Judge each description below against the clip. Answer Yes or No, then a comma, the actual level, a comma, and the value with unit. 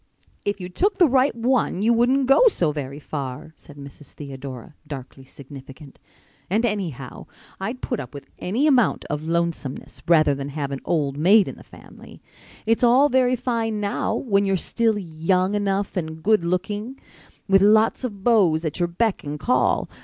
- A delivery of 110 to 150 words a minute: No, average, 175 wpm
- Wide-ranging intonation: Yes, wide, 7.4 semitones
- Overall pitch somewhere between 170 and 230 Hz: Yes, high, 190 Hz